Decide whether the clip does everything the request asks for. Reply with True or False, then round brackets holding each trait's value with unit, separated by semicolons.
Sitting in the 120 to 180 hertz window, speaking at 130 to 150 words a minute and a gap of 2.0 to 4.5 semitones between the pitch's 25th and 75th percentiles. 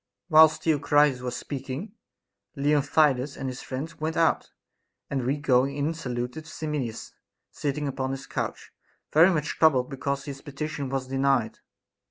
True (140 Hz; 145 wpm; 2.5 semitones)